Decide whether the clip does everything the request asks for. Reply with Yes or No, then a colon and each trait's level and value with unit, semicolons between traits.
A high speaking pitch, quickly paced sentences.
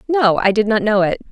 Yes: high, 220 Hz; fast, 275 wpm